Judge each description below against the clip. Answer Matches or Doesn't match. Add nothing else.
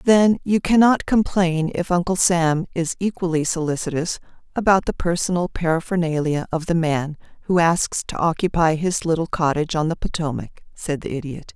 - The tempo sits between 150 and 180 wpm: Matches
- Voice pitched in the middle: Matches